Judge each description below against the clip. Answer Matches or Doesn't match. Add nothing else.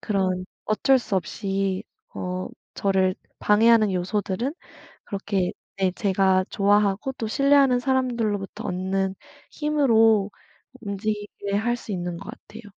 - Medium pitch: Doesn't match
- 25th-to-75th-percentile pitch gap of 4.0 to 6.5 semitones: Doesn't match